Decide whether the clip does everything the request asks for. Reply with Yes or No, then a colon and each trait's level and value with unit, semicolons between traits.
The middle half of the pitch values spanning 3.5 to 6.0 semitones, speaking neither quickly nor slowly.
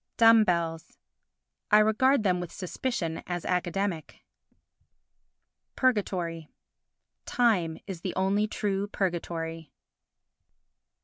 No: average, 4.0 semitones; slow, 85 wpm